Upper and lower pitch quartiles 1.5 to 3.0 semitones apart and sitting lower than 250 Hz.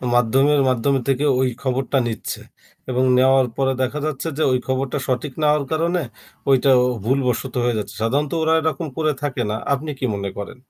Yes: average, 2.7 semitones; low, 135 Hz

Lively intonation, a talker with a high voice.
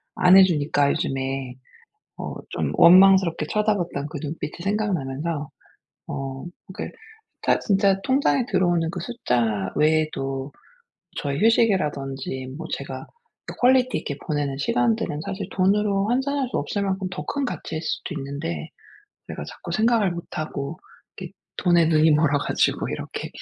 No: wide, 5.7 semitones; medium, 165 Hz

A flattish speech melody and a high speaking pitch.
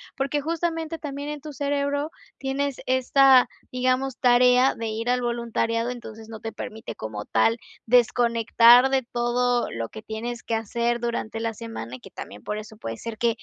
No: average, 3.0 semitones; high, 240 Hz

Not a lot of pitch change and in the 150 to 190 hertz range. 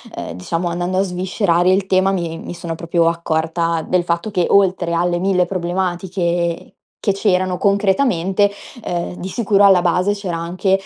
Yes: narrow, 2.1 semitones; medium, 180 Hz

